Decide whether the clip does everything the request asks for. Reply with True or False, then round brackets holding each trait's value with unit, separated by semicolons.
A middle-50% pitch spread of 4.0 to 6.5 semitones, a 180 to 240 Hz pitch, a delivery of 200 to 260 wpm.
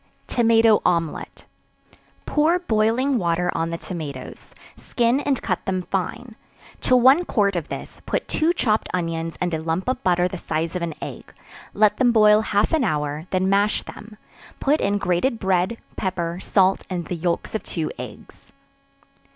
False (5.1 semitones; 190 Hz; 165 wpm)